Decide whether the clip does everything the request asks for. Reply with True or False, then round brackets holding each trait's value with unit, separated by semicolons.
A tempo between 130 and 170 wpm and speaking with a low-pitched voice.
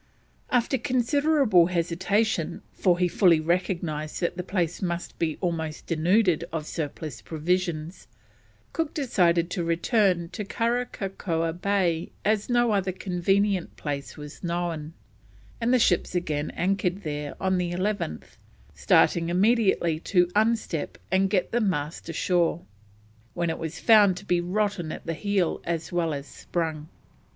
False (140 wpm; 175 Hz)